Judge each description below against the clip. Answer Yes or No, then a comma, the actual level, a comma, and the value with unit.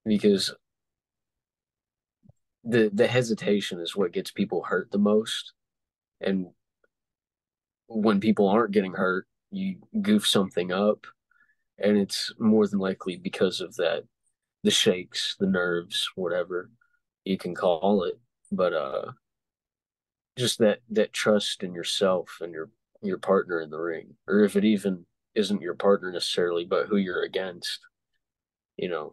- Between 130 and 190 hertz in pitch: No, low, 110 Hz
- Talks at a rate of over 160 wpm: No, average, 140 wpm